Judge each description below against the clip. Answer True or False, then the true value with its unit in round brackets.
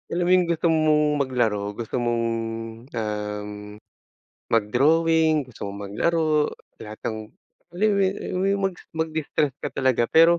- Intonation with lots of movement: True (6.4 semitones)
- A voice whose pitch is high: False (150 Hz)